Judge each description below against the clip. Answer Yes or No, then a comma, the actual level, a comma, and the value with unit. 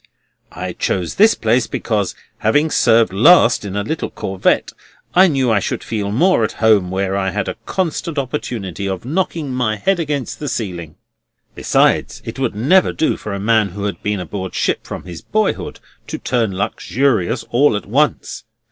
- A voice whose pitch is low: Yes, low, 110 Hz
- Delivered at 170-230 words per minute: Yes, average, 175 wpm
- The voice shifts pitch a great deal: Yes, wide, 6.6 semitones